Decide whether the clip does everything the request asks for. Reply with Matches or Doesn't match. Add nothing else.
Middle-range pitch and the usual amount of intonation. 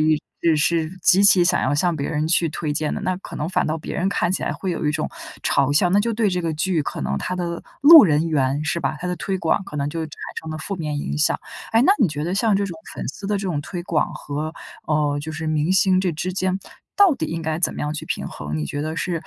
Matches